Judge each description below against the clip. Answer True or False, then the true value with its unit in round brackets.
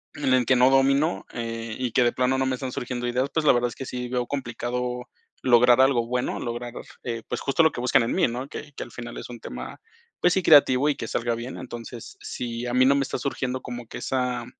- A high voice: False (125 Hz)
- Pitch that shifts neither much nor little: False (1.7 semitones)